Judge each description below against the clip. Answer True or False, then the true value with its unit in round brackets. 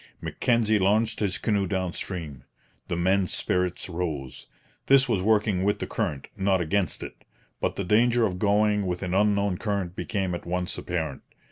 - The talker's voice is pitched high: False (95 Hz)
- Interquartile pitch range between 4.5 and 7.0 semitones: False (2.8 semitones)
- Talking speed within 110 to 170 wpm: True (165 wpm)